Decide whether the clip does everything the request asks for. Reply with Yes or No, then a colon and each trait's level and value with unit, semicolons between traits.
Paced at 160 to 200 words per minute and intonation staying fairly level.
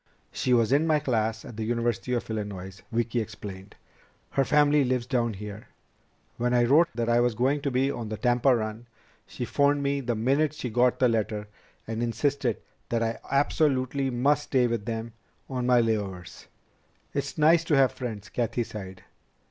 No: average, 180 wpm; average, 3.4 semitones